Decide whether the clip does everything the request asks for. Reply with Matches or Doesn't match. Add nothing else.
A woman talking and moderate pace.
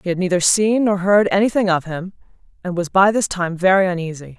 Doesn't match